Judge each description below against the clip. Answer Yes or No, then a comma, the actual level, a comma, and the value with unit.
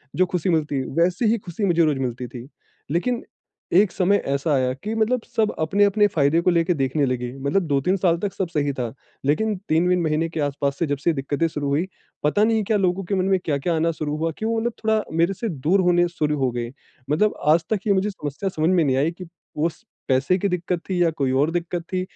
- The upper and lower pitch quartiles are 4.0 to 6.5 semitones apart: Yes, average, 4.9 semitones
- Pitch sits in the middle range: Yes, medium, 170 Hz